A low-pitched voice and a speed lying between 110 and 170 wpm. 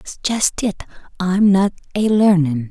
No: high, 190 Hz; slow, 135 wpm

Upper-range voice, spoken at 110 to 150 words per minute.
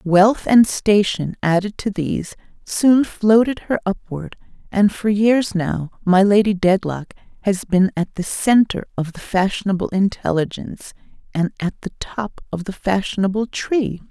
Yes: high, 200 Hz; average, 145 wpm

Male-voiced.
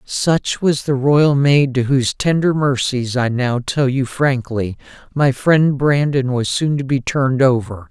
Yes: male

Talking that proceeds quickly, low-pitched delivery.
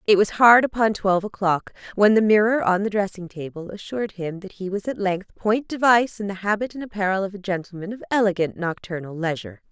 No: fast, 210 wpm; high, 200 Hz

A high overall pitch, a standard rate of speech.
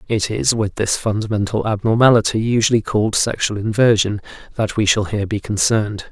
No: low, 105 Hz; average, 155 wpm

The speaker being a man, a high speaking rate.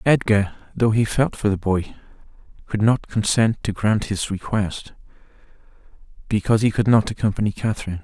No: male; average, 150 wpm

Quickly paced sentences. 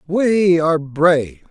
No: slow, 120 wpm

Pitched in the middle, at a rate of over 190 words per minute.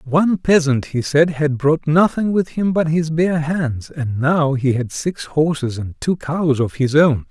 Yes: medium, 150 Hz; fast, 205 wpm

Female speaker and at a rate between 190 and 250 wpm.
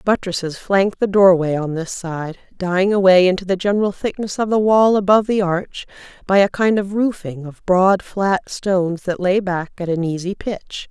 Yes: female; average, 195 wpm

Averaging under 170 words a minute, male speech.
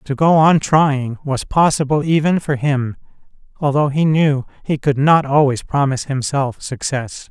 Yes: average, 155 wpm; male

